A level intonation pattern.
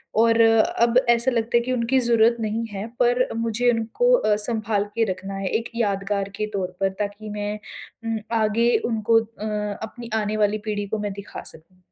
Yes: narrow, 2.2 semitones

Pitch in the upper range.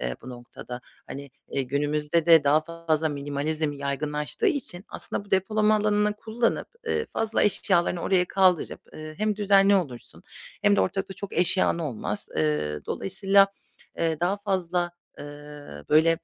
No: medium, 165 Hz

